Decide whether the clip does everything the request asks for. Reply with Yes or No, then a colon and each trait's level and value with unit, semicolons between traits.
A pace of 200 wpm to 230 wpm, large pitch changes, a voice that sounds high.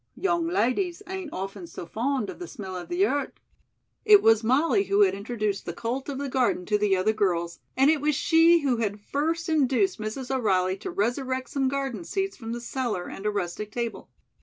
Yes: fast, 205 wpm; wide, 6.8 semitones; very high, 250 Hz